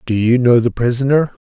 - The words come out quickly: Yes, fast, 210 wpm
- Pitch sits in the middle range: No, low, 125 Hz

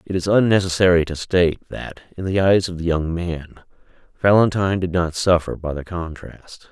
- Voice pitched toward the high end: No, very low, 90 Hz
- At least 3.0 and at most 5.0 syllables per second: No, 5.3 syllables/s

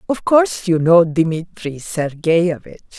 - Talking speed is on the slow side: Yes, slow, 120 wpm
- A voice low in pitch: No, medium, 175 Hz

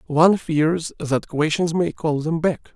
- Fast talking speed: No, average, 175 wpm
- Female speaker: No, male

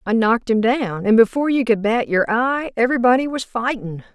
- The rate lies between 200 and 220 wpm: Yes, fast, 205 wpm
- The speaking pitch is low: No, high, 235 Hz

